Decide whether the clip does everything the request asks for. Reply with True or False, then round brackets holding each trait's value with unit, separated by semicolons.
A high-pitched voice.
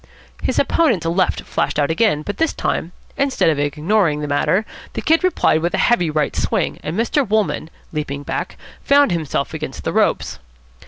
False (170 Hz)